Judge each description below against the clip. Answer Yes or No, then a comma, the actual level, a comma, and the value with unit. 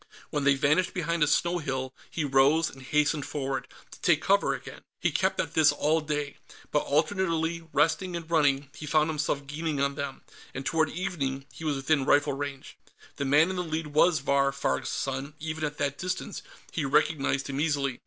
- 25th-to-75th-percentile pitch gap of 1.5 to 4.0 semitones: Yes, narrow, 2.6 semitones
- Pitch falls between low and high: Yes, medium, 150 Hz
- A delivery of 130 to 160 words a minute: No, average, 195 wpm